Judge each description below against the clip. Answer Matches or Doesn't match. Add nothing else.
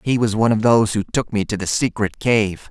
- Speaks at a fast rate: Matches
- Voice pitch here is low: Matches